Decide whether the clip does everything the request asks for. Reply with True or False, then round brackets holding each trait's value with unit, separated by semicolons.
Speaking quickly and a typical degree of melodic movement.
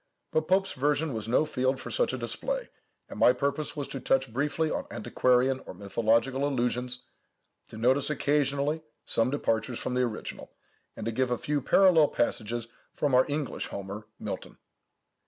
False (165 wpm; 3.6 semitones)